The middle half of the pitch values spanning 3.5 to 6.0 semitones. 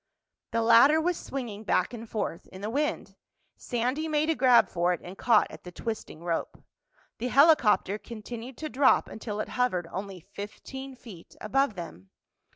Yes: average, 5.1 semitones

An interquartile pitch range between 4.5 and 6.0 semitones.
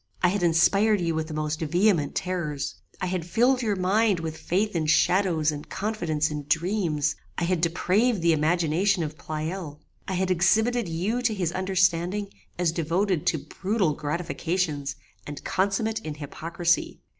No: average, 3.7 semitones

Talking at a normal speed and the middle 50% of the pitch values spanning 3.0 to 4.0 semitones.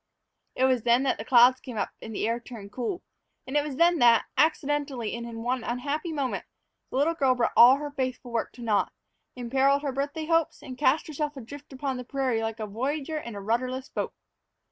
No: fast, 210 wpm; average, 3.5 semitones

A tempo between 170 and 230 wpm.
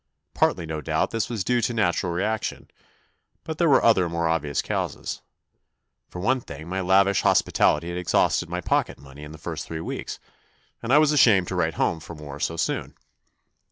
Yes: average, 190 wpm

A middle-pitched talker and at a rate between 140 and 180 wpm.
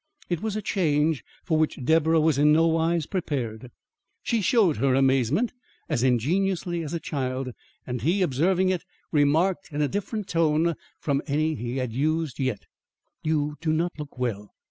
Yes: medium, 155 Hz; average, 165 wpm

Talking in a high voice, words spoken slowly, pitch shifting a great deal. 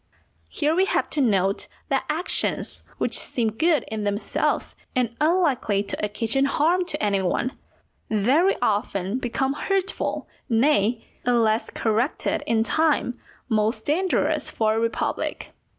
Yes: high, 235 Hz; slow, 130 wpm; wide, 5.8 semitones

